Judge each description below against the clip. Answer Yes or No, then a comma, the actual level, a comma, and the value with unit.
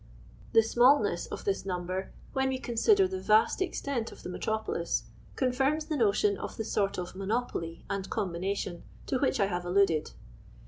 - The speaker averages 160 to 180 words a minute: Yes, average, 165 wpm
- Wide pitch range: Yes, wide, 5.9 semitones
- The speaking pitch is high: Yes, high, 220 Hz